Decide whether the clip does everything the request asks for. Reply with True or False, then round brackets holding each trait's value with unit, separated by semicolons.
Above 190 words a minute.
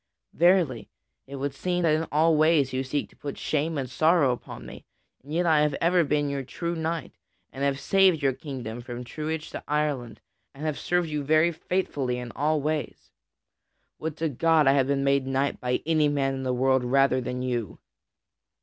True (200 wpm)